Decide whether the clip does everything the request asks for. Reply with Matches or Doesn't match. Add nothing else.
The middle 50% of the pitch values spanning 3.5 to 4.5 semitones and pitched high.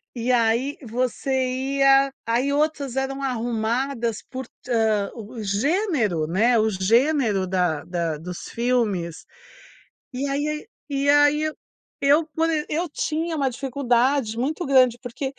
Matches